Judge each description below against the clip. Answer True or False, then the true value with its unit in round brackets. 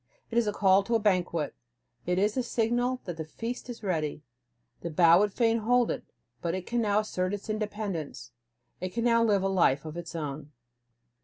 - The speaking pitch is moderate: False (200 Hz)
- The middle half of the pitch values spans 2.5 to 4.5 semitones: False (5.1 semitones)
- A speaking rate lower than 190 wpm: False (205 wpm)